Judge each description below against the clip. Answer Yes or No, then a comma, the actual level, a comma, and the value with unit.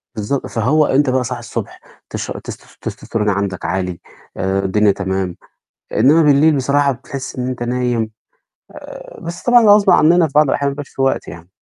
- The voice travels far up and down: Yes, wide, 6.3 semitones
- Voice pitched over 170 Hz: No, low, 130 Hz